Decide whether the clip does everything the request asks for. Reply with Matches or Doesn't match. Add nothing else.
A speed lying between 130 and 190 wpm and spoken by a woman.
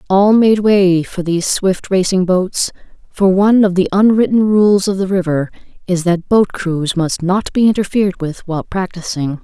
Matches